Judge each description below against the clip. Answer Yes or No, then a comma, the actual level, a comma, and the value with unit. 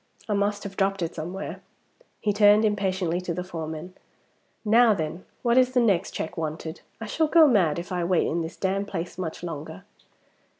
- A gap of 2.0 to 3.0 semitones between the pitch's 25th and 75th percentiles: No, average, 3.8 semitones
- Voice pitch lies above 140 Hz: Yes, medium, 185 Hz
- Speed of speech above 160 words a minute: Yes, average, 185 wpm